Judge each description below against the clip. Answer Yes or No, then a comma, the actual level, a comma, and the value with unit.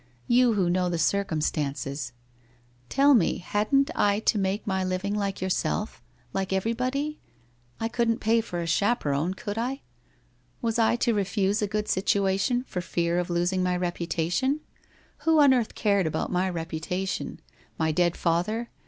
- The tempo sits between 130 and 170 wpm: Yes, average, 155 wpm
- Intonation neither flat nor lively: Yes, average, 4.6 semitones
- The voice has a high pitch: Yes, high, 195 Hz